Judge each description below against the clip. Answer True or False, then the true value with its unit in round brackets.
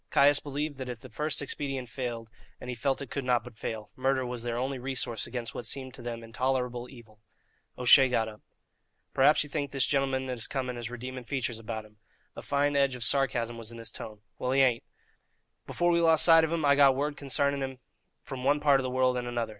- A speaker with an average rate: False (230 wpm)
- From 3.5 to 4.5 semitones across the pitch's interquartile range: False (2.7 semitones)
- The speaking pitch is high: False (130 Hz)